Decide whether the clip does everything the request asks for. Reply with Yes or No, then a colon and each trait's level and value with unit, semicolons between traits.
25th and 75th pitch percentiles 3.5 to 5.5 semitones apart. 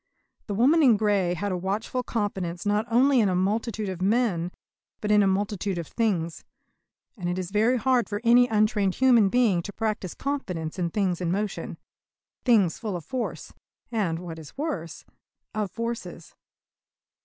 Yes: average, 4.3 semitones